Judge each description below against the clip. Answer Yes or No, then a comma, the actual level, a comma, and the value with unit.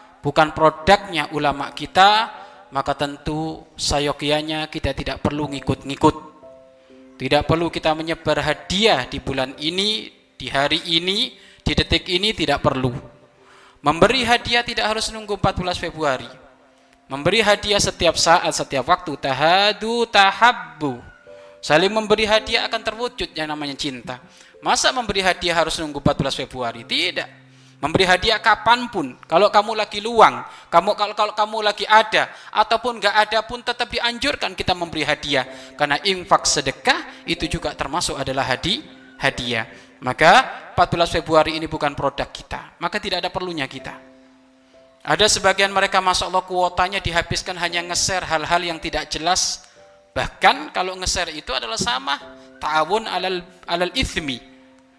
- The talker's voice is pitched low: No, medium, 165 Hz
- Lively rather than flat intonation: Yes, wide, 5.8 semitones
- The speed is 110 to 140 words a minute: Yes, average, 135 wpm